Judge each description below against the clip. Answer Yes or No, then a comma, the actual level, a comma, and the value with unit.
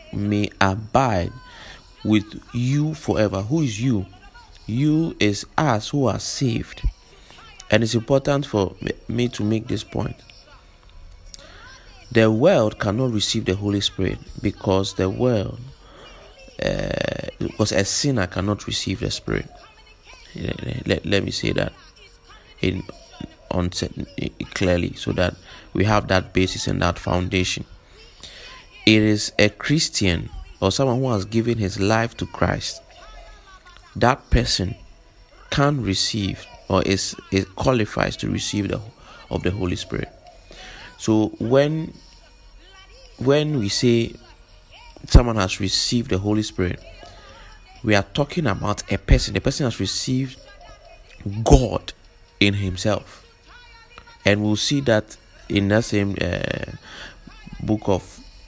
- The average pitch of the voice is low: Yes, low, 105 Hz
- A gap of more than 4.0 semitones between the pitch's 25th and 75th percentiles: Yes, average, 4.8 semitones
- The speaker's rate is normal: No, slow, 125 wpm